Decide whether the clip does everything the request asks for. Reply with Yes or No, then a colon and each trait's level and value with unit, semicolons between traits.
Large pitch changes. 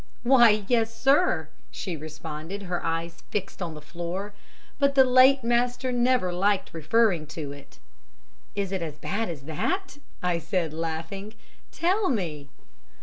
Yes: wide, 6.8 semitones